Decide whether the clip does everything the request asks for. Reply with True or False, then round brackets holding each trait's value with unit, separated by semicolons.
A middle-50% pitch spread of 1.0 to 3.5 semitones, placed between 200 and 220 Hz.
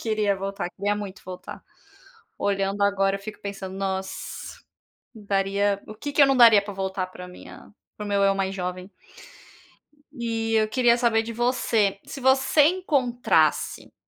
True (3.0 semitones; 205 Hz)